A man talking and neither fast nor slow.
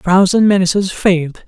Yes: male; average, 165 wpm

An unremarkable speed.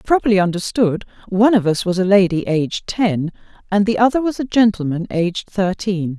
Yes: average, 175 wpm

